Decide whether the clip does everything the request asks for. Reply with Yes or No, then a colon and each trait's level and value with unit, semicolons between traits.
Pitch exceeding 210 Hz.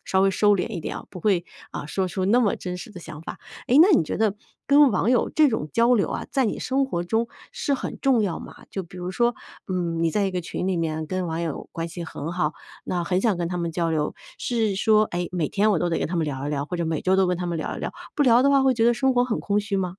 No: medium, 185 Hz